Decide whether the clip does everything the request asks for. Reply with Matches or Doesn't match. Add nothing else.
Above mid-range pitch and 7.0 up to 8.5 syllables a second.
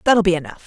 Matches